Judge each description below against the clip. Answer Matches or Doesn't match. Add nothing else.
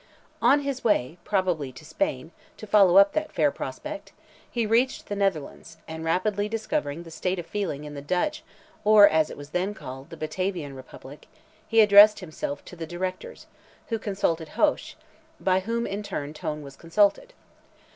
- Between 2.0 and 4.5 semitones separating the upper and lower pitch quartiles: Doesn't match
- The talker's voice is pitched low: Doesn't match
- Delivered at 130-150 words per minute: Doesn't match